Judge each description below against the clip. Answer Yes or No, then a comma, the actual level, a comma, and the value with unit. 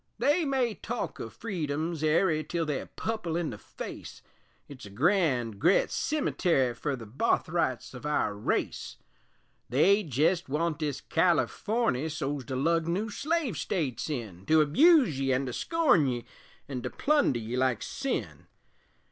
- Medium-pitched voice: Yes, medium, 155 Hz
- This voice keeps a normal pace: Yes, average, 150 wpm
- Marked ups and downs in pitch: Yes, wide, 6.8 semitones